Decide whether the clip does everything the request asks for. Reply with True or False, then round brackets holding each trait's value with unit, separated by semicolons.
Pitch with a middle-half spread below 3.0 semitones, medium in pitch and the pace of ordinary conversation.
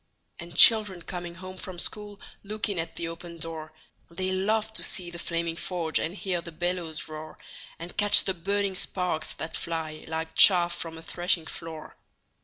True (2.4 semitones; 175 Hz; 180 wpm)